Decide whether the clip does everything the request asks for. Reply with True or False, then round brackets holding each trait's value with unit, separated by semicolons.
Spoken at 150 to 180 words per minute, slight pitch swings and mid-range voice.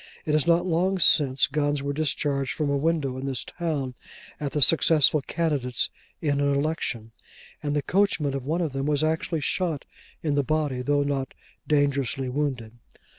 True (175 wpm; 2.3 semitones; 145 Hz)